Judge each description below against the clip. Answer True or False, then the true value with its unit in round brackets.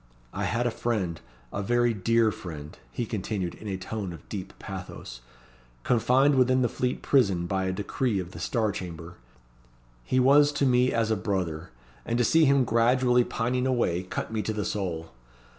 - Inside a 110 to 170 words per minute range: False (180 wpm)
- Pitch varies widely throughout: False (4.8 semitones)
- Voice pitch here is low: True (110 Hz)